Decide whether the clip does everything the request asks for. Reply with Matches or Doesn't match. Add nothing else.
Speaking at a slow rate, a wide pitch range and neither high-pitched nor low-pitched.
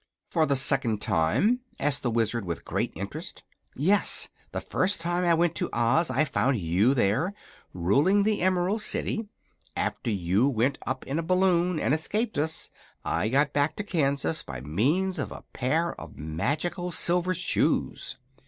Doesn't match